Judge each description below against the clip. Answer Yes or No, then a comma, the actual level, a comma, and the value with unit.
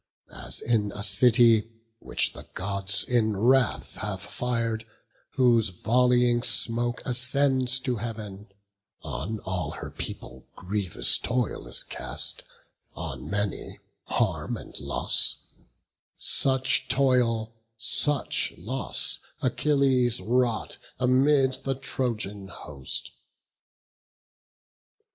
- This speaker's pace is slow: Yes, slow, 95 wpm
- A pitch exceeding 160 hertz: No, low, 120 Hz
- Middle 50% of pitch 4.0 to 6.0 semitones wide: No, average, 3.6 semitones